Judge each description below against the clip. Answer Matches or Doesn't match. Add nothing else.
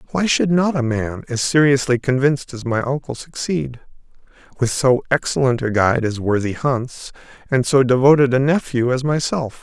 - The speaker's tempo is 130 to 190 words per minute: Matches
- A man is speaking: Matches